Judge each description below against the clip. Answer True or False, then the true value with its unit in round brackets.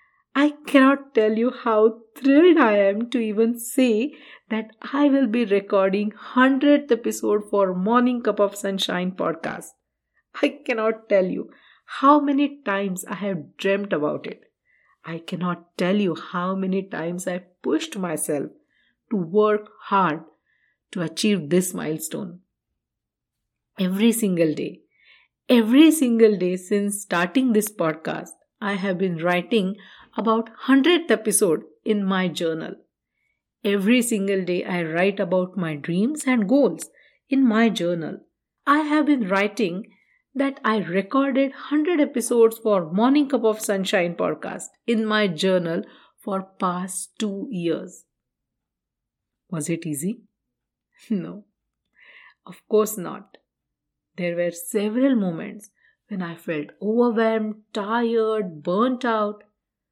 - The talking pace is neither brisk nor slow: False (125 wpm)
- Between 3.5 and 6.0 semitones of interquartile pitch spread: True (4.7 semitones)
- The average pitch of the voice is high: True (210 Hz)